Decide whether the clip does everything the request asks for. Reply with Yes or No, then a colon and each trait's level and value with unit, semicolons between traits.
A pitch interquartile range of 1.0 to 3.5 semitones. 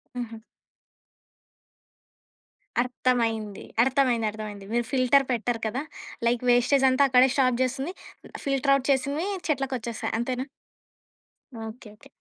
Yes: narrow, 2.5 semitones